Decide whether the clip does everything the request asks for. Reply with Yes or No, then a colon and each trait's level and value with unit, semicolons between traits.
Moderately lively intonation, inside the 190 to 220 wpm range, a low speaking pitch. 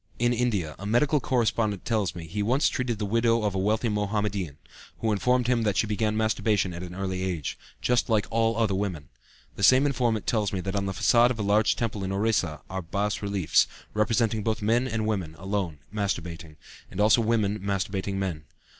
Yes: average, 3.0 semitones; average, 200 wpm; low, 105 Hz